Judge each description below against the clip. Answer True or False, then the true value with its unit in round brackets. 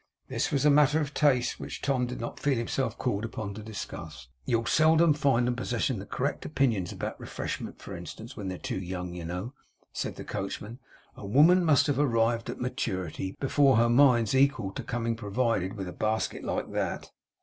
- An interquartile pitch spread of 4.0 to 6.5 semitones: True (5.1 semitones)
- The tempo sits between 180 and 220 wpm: True (190 wpm)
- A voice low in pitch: True (120 Hz)